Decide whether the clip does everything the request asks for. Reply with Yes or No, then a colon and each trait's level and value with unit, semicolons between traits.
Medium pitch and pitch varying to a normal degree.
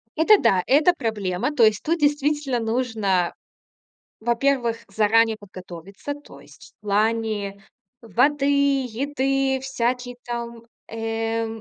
No: high, 235 Hz; average, 4.0 semitones